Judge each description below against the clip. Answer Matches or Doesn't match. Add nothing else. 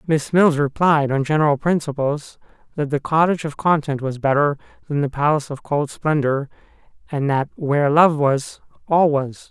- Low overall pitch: Doesn't match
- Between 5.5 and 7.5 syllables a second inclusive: Doesn't match